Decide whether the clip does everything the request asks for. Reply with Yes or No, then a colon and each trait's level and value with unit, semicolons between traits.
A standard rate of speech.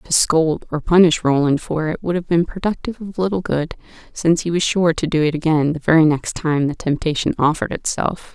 No: fast, 215 wpm